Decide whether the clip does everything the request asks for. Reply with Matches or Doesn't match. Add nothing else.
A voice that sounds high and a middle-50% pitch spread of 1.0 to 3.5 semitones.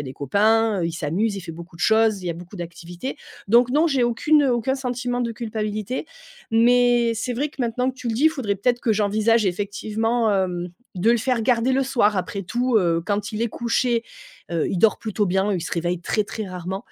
Doesn't match